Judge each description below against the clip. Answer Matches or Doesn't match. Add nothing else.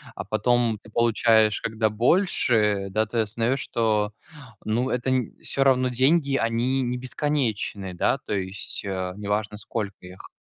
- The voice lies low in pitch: Matches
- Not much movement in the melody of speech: Doesn't match